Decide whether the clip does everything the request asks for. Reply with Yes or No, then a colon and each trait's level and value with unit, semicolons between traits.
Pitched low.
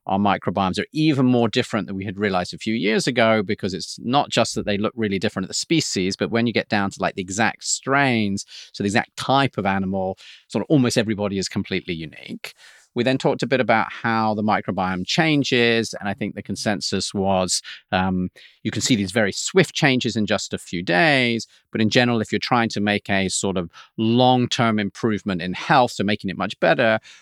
Yes: low, 110 Hz